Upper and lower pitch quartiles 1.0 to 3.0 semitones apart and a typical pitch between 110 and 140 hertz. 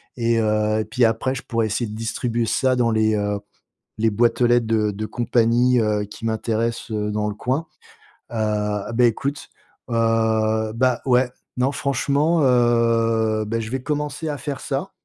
Yes: narrow, 2.4 semitones; low, 115 Hz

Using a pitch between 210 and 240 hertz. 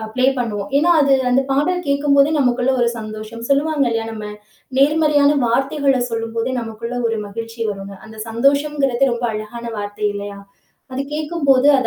No: very high, 250 Hz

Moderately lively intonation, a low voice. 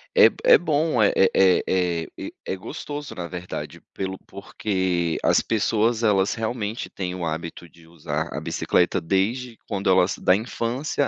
Yes: average, 4.4 semitones; very low, 95 Hz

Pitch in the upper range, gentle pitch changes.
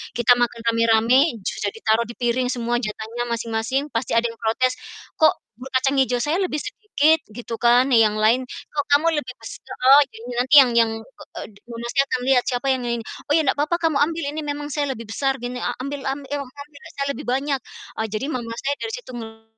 No: very high, 255 Hz; average, 3.5 semitones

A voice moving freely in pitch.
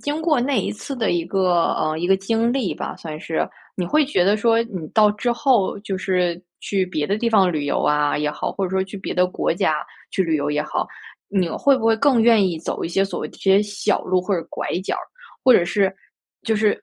No: average, 4.4 semitones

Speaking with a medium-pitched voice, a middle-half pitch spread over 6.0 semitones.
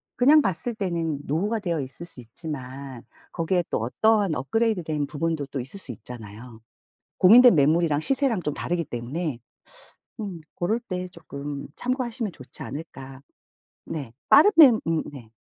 Yes: medium, 165 Hz; wide, 7.2 semitones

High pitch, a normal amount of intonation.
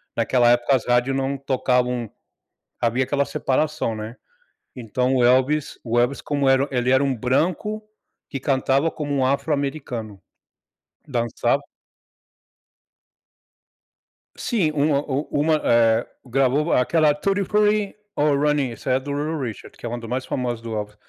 No: low, 135 Hz; average, 3.3 semitones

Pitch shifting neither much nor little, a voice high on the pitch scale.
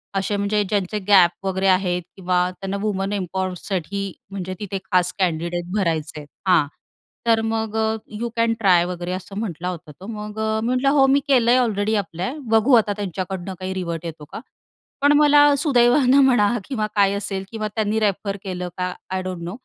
Yes: average, 3.3 semitones; high, 195 Hz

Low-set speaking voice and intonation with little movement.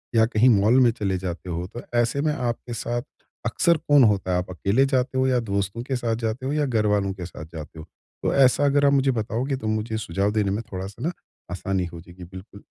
No: low, 110 Hz; average, 5.2 semitones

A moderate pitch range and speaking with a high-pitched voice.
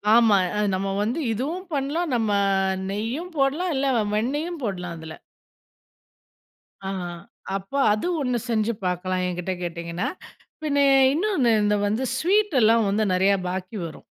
No: wide, 7.0 semitones; high, 220 Hz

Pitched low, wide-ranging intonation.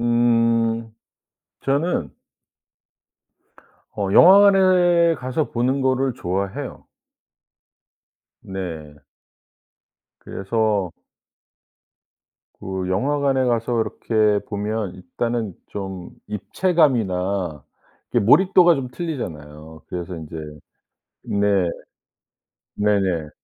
Yes: low, 110 Hz; wide, 6.0 semitones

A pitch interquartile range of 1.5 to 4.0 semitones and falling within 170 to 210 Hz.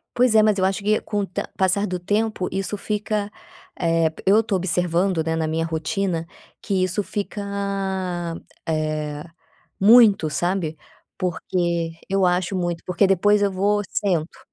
Yes: average, 3.5 semitones; medium, 185 Hz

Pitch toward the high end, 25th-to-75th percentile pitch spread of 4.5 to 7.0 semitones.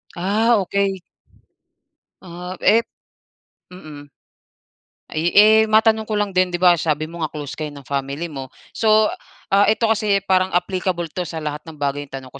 No: medium, 180 Hz; average, 5.1 semitones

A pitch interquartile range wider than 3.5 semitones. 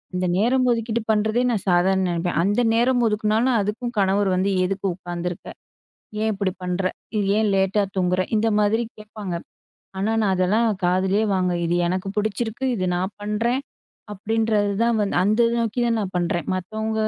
No: average, 3.0 semitones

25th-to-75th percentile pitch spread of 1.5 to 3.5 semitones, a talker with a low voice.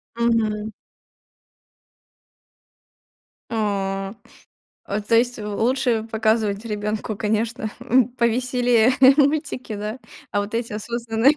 No: narrow, 2.4 semitones; high, 225 Hz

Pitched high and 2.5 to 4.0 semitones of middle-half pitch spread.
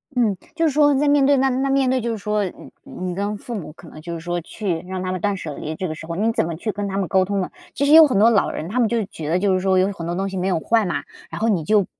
No: high, 200 Hz; average, 4.7 semitones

